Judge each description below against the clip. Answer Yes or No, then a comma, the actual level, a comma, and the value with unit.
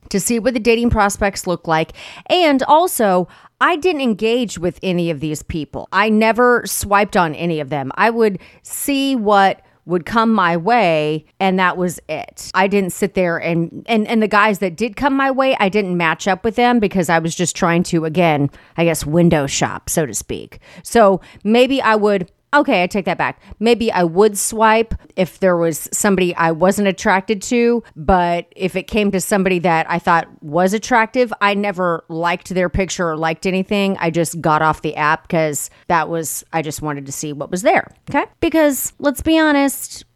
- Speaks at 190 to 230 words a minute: Yes, average, 200 wpm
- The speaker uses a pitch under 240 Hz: Yes, high, 190 Hz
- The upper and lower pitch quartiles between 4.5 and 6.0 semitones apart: Yes, average, 5.0 semitones